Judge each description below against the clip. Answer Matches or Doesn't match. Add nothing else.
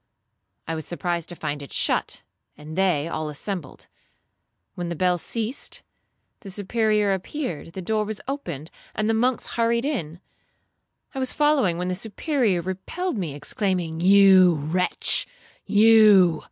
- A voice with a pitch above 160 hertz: Matches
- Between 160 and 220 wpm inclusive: Doesn't match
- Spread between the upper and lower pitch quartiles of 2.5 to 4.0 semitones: Doesn't match